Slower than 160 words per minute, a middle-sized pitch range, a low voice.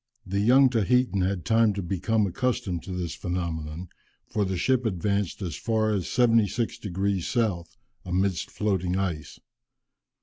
Yes: average, 140 wpm; average, 3.8 semitones; low, 100 Hz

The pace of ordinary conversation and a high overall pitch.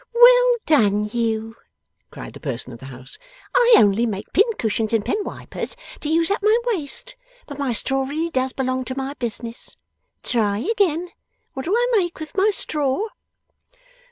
Yes: average, 165 wpm; very high, 270 Hz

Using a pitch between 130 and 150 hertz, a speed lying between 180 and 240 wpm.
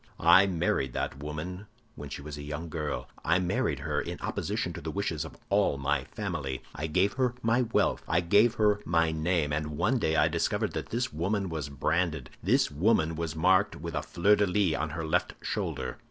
No: very low, 80 Hz; average, 200 wpm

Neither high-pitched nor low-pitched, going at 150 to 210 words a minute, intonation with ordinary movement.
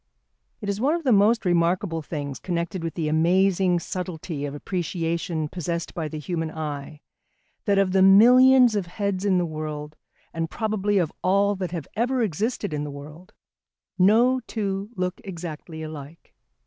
Yes: medium, 180 Hz; average, 160 wpm; average, 4.1 semitones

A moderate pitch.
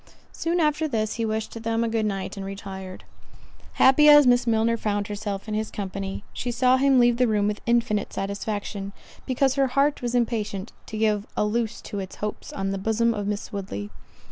No: high, 220 Hz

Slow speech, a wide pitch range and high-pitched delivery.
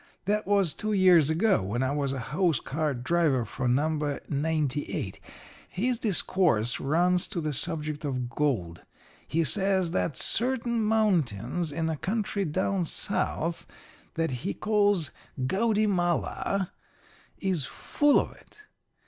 No: slow, 130 wpm; wide, 5.7 semitones; medium, 165 Hz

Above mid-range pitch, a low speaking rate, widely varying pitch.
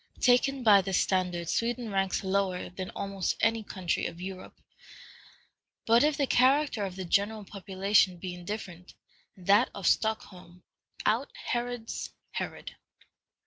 No: high, 200 Hz; slow, 130 wpm; average, 3.7 semitones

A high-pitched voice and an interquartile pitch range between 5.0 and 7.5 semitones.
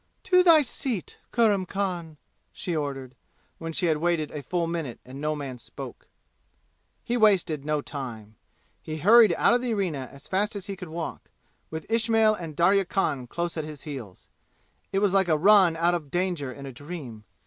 No: medium, 170 Hz; average, 5.3 semitones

